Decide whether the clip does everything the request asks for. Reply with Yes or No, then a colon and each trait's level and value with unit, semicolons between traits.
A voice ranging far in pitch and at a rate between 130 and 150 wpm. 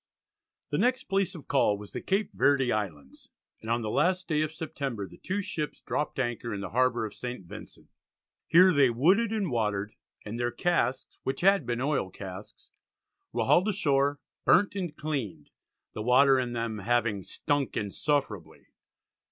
No: wide, 6.5 semitones; average, 170 wpm